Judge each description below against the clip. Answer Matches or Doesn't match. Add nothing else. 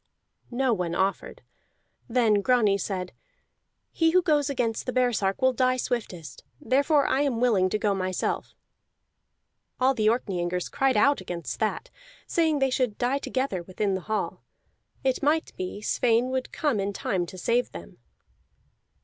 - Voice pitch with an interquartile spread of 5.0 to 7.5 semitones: Matches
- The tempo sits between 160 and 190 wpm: Doesn't match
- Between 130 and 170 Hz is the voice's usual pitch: Doesn't match